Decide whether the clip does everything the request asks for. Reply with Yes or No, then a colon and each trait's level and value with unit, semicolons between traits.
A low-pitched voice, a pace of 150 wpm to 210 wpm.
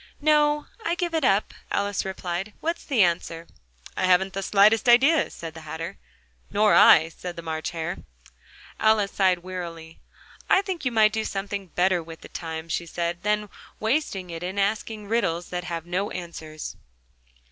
No: high, 190 Hz; average, 170 wpm